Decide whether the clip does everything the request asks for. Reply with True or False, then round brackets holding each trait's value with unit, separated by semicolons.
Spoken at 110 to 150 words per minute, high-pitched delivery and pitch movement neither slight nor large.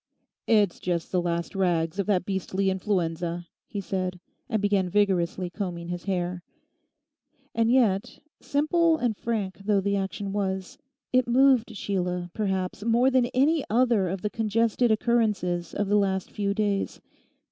True (145 wpm; 200 Hz; 3.6 semitones)